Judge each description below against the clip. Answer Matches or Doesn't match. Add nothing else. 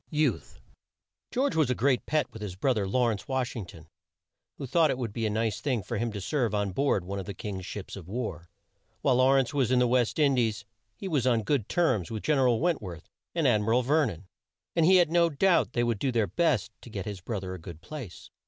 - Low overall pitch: Matches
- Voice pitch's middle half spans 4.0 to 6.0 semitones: Matches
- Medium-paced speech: Doesn't match